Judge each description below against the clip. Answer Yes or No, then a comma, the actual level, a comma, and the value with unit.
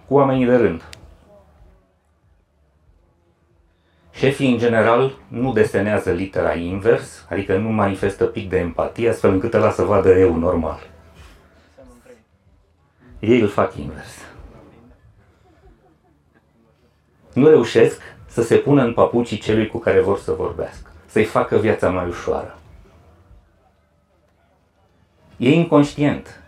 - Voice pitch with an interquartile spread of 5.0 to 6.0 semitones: Yes, wide, 5.5 semitones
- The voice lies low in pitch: Yes, very low, 95 Hz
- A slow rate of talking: Yes, slow, 110 wpm